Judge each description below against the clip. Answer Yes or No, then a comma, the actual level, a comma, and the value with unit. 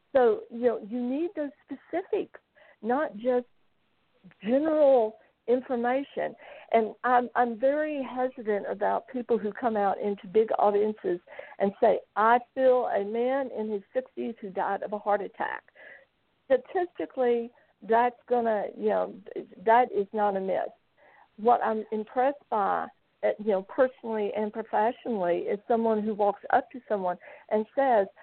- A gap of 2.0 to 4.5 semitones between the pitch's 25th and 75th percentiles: Yes, average, 3.6 semitones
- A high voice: Yes, high, 240 Hz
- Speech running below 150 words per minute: Yes, average, 140 wpm